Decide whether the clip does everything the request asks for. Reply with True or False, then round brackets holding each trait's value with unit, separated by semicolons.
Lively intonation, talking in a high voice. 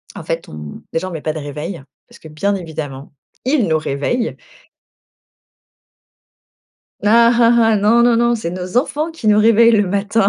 True (6.7 semitones; 205 Hz)